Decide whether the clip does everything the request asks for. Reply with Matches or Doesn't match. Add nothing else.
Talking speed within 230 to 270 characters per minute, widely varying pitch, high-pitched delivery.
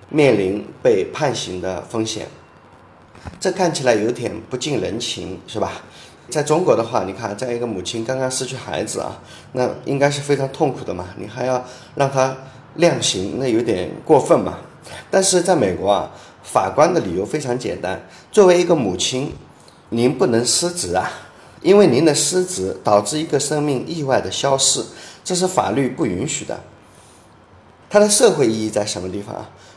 Doesn't match